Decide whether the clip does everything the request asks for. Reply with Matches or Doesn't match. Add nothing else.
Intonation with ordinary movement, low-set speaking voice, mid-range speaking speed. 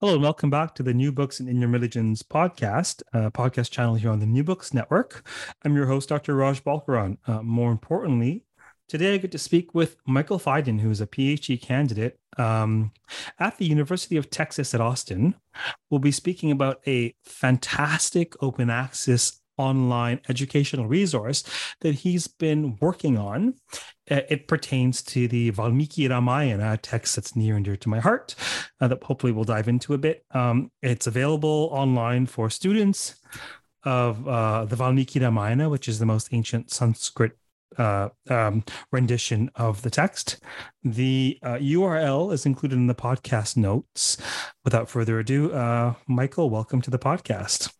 Matches